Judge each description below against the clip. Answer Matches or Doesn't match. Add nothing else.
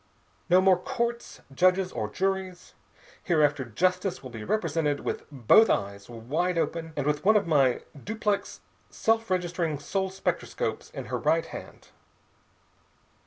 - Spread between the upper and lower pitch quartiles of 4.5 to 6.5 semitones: Matches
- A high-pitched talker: Doesn't match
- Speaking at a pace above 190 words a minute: Doesn't match